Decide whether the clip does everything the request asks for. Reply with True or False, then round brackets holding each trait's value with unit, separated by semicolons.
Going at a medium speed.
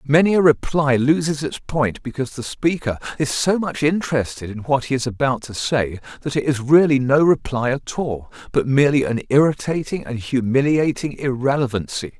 True (170 wpm)